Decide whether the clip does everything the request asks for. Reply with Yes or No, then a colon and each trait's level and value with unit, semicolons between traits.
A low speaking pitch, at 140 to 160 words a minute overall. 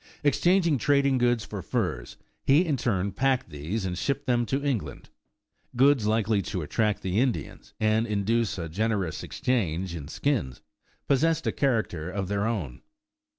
Yes: low, 110 Hz; average, 150 wpm